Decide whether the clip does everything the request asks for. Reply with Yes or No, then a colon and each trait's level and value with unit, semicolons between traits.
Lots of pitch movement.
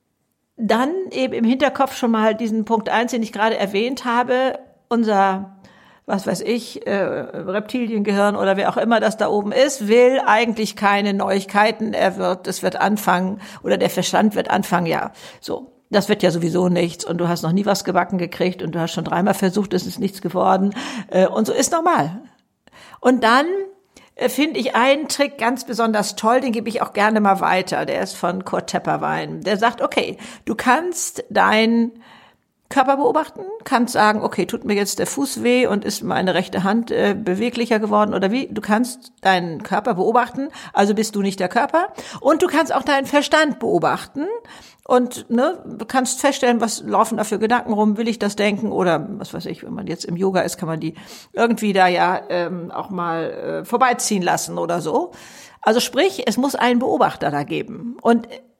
No: average, 4.2 semitones